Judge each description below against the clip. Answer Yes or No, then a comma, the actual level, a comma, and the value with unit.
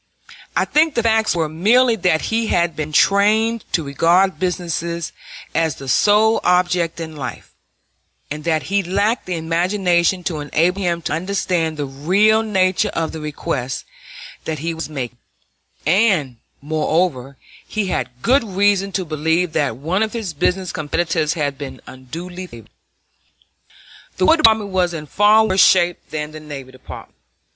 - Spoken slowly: No, average, 155 wpm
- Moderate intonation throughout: Yes, average, 4.3 semitones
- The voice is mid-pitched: Yes, medium, 175 Hz